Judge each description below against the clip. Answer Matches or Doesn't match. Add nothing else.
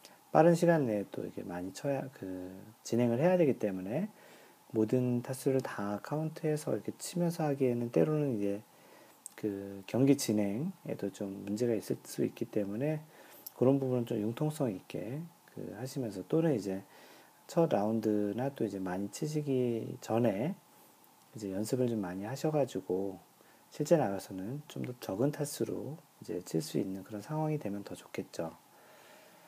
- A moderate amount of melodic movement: Doesn't match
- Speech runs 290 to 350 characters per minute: Matches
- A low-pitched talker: Matches